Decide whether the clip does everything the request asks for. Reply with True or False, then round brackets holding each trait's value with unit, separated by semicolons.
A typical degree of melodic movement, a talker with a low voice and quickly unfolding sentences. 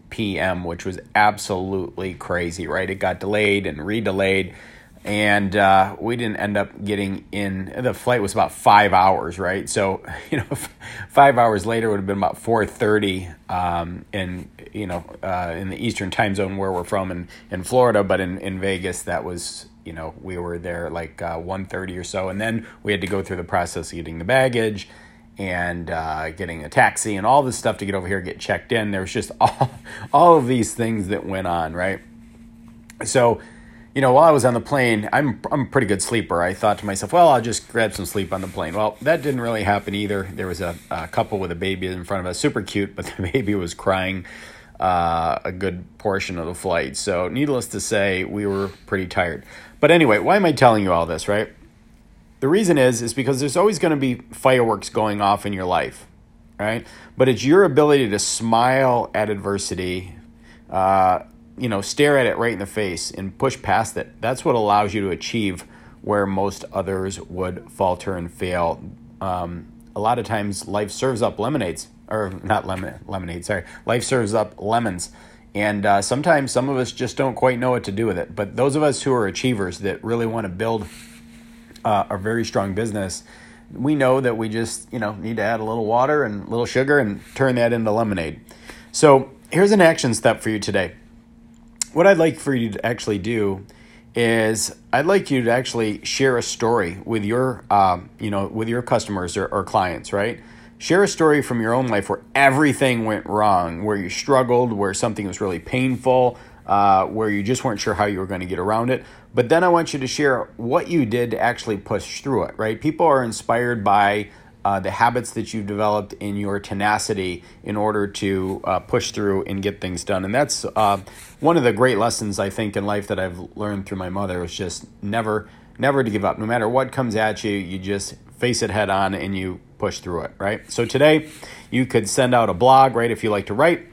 True (3.7 semitones; 105 Hz; 215 wpm)